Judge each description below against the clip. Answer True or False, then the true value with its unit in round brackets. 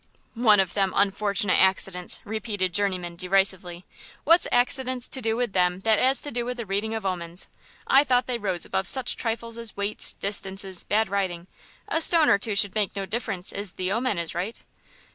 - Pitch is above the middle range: True (205 Hz)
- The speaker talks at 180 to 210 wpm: True (190 wpm)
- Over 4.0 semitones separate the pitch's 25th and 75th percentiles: False (3.7 semitones)